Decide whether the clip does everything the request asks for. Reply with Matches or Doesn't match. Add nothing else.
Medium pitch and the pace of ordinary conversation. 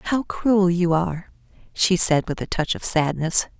Matches